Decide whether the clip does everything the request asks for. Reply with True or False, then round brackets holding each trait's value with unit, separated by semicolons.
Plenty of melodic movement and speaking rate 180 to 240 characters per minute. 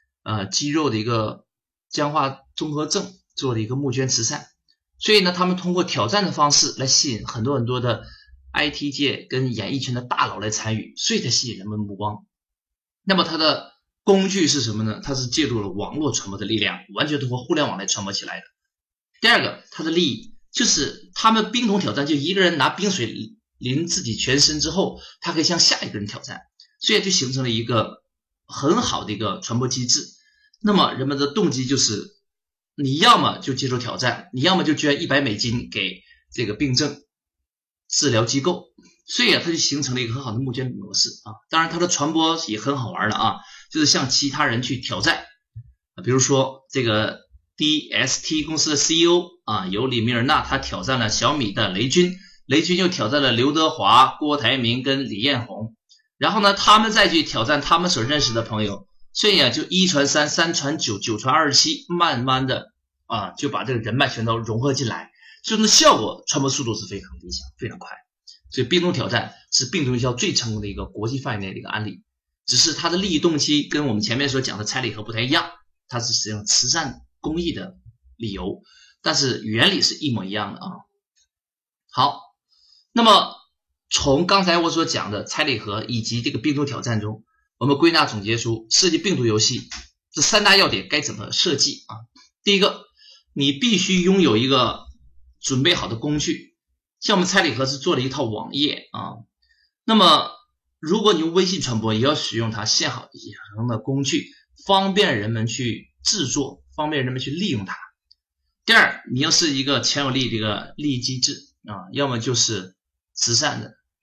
False (7.2 semitones; 290 characters per minute)